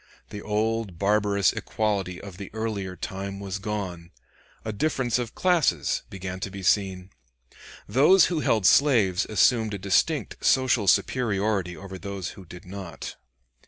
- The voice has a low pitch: Yes, low, 100 Hz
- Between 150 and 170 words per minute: No, average, 140 wpm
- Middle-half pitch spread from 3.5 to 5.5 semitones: No, average, 2.8 semitones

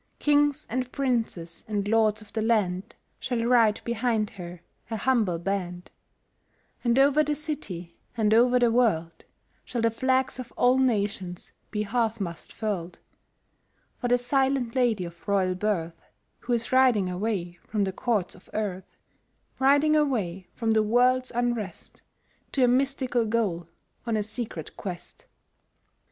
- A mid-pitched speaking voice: No, high, 225 Hz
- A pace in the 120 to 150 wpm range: Yes, average, 145 wpm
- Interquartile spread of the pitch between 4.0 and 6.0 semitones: Yes, average, 4.7 semitones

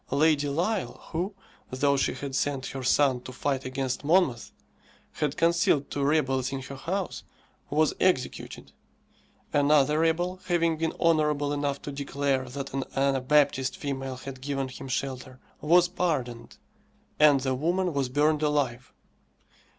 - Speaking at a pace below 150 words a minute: Yes, average, 140 wpm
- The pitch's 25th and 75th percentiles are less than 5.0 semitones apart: Yes, average, 2.8 semitones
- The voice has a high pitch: No, medium, 140 Hz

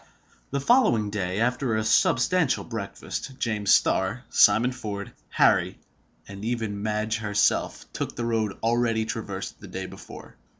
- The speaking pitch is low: Yes, low, 110 Hz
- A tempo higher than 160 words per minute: No, slow, 135 wpm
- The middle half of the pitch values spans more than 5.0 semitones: No, average, 3.0 semitones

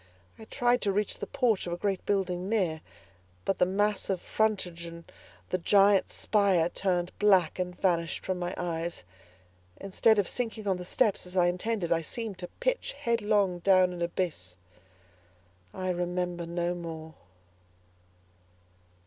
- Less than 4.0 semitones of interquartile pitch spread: Yes, average, 2.8 semitones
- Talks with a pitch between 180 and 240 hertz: Yes, medium, 185 Hz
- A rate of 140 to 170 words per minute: Yes, average, 150 wpm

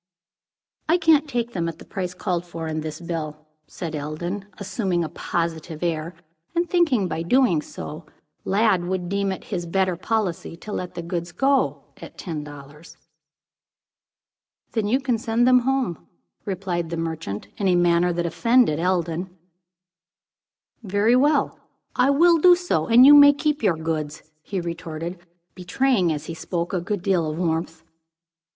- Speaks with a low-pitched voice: No, medium, 180 Hz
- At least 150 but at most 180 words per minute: Yes, average, 160 wpm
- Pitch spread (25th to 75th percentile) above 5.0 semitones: Yes, wide, 5.6 semitones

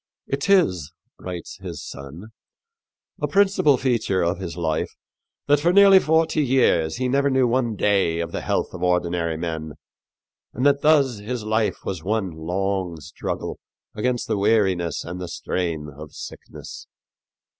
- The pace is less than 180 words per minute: Yes, average, 150 wpm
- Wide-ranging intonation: Yes, wide, 7.4 semitones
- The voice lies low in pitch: Yes, low, 100 Hz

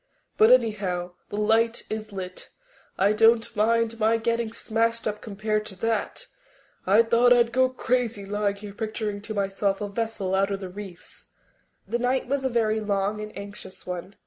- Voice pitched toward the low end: No, high, 215 Hz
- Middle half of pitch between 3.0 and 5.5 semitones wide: No, narrow, 2.4 semitones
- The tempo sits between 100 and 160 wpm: No, average, 170 wpm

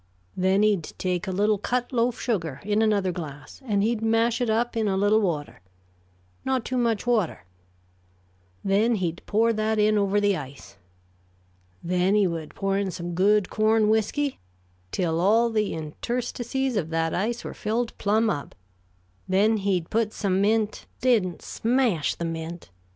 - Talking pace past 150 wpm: Yes, average, 160 wpm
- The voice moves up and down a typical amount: Yes, average, 3.7 semitones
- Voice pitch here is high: Yes, high, 210 Hz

